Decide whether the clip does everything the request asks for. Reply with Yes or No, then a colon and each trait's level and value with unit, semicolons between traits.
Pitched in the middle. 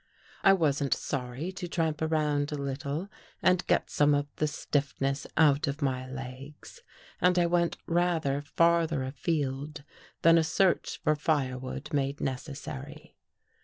Yes: medium, 150 Hz